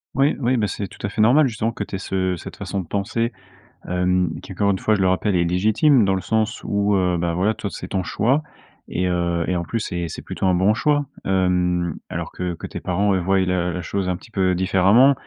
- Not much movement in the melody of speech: No, average, 3.1 semitones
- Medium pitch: No, very low, 95 Hz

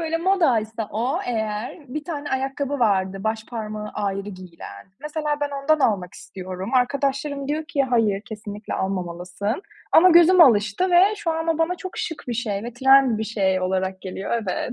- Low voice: No, high, 230 Hz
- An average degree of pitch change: No, wide, 6.6 semitones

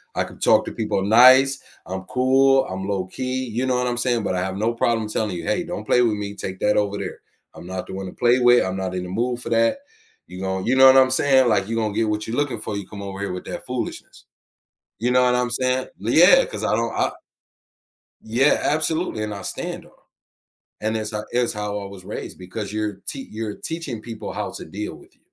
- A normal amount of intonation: Yes, average, 4.0 semitones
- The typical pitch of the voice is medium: No, low, 110 Hz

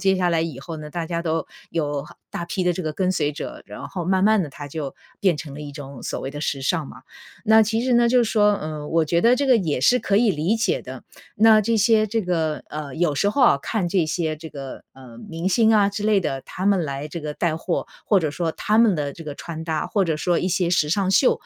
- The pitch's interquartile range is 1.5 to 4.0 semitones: No, average, 5.1 semitones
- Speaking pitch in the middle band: Yes, medium, 170 Hz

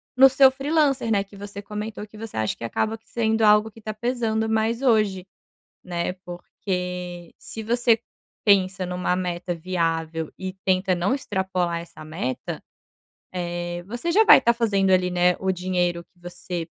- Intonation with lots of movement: No, average, 3.8 semitones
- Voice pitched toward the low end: No, high, 190 Hz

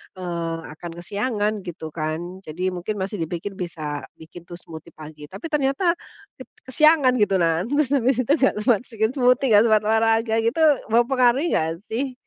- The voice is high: Yes, high, 215 Hz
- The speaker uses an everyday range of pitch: No, wide, 6.6 semitones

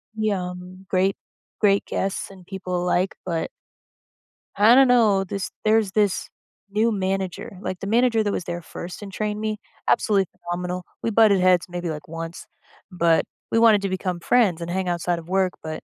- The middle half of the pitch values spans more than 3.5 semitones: No, average, 2.8 semitones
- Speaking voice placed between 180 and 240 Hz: Yes, high, 190 Hz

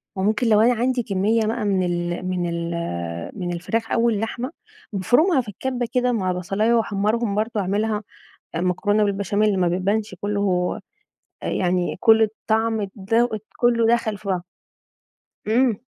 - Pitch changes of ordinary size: Yes, average, 3.5 semitones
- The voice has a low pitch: No, high, 210 Hz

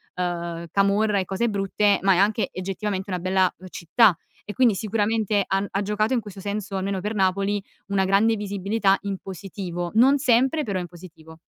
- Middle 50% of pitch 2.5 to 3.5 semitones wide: No, narrow, 2.1 semitones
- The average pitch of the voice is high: Yes, high, 195 Hz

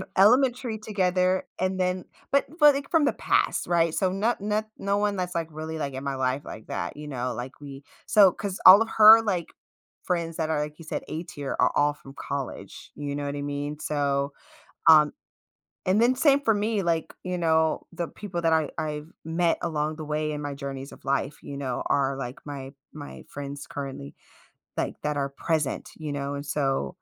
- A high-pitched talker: No, medium, 155 Hz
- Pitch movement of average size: Yes, average, 4.7 semitones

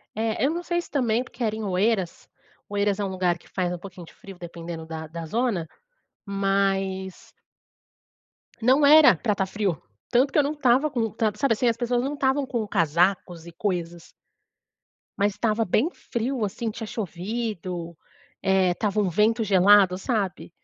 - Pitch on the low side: No, high, 205 Hz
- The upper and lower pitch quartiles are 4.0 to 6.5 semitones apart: Yes, average, 4.5 semitones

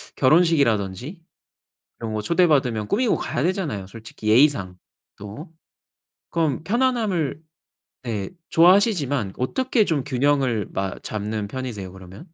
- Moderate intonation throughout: No, wide, 7.8 semitones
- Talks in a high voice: No, low, 130 Hz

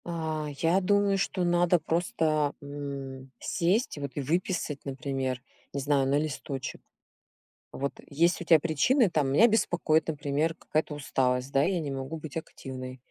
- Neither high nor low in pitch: Yes, medium, 150 Hz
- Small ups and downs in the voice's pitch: No, average, 3.7 semitones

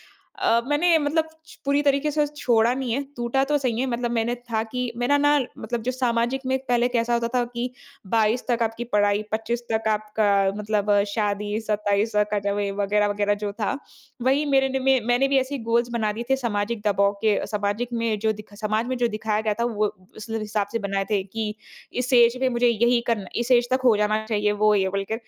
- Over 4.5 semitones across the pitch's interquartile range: No, average, 3.0 semitones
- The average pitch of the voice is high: Yes, high, 230 Hz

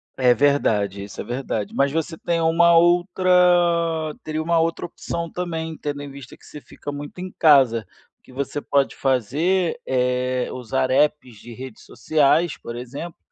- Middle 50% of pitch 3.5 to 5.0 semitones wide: Yes, average, 4.7 semitones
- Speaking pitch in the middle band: Yes, medium, 145 Hz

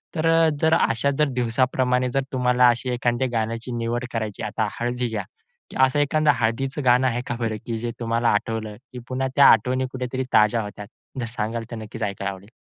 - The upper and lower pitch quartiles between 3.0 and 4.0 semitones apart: No, narrow, 2.5 semitones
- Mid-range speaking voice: No, low, 120 Hz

